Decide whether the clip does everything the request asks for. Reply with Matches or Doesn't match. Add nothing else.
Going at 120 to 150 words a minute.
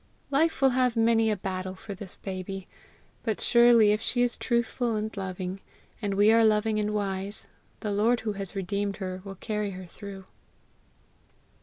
Doesn't match